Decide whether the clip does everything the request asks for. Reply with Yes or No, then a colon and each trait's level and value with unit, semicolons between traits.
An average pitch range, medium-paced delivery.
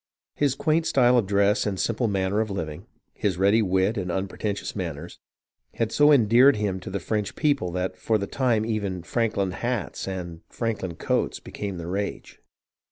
Yes: average, 3.5 semitones; average, 170 wpm